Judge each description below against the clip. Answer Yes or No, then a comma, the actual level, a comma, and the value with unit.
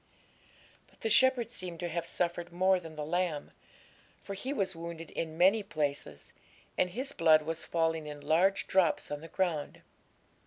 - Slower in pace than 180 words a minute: Yes, average, 165 wpm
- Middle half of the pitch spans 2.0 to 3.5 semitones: Yes, average, 3.1 semitones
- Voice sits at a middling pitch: Yes, medium, 170 Hz